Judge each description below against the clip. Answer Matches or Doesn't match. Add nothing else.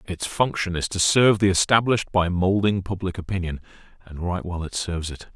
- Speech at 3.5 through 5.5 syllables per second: Doesn't match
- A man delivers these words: Matches